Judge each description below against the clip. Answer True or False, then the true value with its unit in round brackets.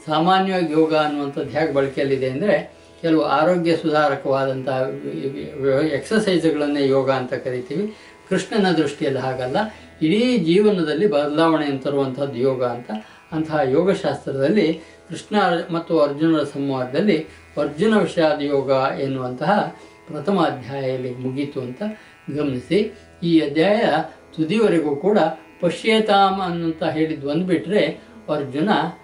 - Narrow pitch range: False (3.9 semitones)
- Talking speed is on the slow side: False (95 wpm)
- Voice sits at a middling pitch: True (155 Hz)